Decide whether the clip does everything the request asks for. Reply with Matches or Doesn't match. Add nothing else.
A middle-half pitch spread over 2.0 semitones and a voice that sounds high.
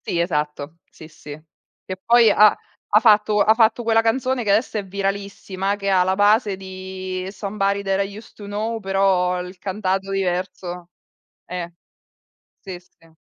Matches